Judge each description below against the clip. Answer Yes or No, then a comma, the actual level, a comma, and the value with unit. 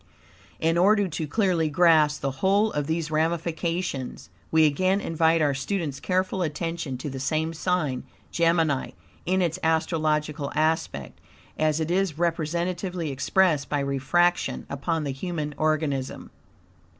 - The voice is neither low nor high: Yes, medium, 160 Hz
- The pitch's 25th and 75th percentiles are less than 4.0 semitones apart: Yes, average, 2.9 semitones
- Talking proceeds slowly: Yes, slow, 130 wpm